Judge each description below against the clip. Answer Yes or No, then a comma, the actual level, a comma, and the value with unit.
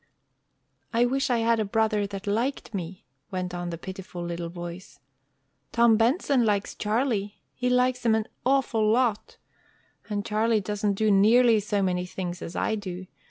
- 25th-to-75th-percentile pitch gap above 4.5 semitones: No, average, 3.7 semitones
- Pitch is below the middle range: No, high, 210 Hz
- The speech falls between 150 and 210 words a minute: Yes, average, 160 wpm